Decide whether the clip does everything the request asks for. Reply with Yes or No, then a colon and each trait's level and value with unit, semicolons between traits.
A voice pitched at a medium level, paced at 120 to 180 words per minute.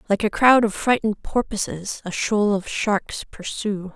No: high, 210 Hz; average, 165 wpm